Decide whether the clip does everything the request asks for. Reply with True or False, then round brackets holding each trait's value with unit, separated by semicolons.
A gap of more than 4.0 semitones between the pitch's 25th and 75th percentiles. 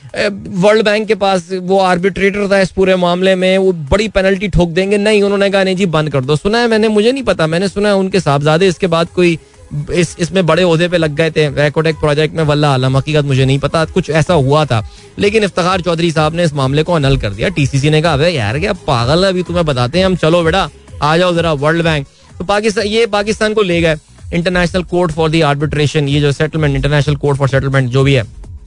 True (4.5 semitones)